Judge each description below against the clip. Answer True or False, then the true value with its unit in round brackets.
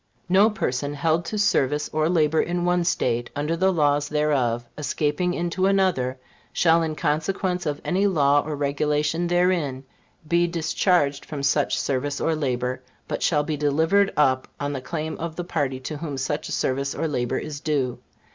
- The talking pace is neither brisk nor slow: True (170 wpm)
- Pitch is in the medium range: True (150 Hz)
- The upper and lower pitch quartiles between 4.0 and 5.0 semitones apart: False (3.5 semitones)